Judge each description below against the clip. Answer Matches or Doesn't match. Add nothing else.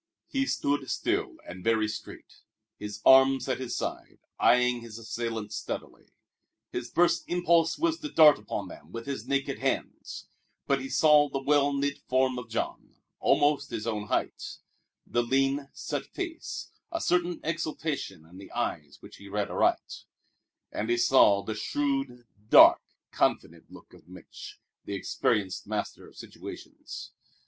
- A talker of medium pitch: Doesn't match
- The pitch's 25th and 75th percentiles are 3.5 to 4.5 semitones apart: Doesn't match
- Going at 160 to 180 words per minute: Doesn't match